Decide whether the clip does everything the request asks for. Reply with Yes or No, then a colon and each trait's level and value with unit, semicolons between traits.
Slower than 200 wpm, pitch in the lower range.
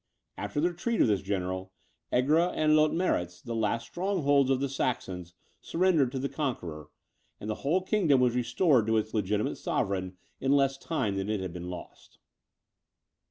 Yes: average, 165 wpm; low, 125 Hz